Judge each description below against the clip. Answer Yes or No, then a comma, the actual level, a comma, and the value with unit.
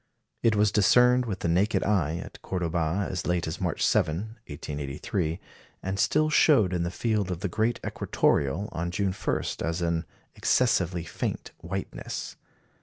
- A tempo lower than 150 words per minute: No, average, 155 wpm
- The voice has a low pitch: Yes, very low, 90 Hz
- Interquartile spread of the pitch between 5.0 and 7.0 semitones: No, average, 4.0 semitones